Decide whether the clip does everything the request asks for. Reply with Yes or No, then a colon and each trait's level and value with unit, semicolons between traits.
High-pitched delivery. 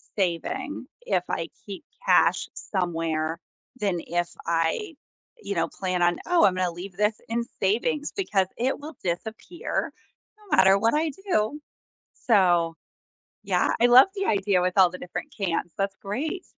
Yes: high, 195 Hz